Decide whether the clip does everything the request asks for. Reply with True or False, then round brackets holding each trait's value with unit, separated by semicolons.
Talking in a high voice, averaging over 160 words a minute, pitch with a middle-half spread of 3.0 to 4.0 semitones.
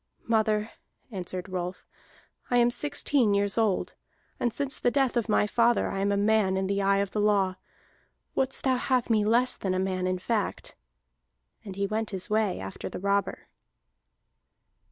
True (210 Hz; 175 wpm; 3.5 semitones)